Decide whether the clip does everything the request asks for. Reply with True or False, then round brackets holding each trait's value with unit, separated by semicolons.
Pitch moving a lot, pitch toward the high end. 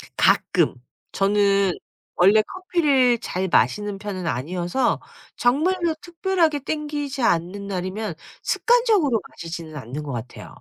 True (8.8 semitones; 210 Hz)